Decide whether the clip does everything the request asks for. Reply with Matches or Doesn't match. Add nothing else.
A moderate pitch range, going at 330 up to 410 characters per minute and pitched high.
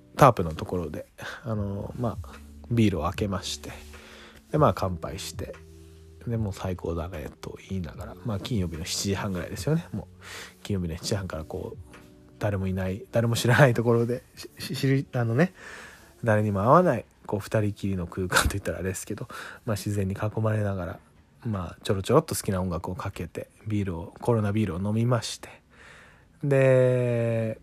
Doesn't match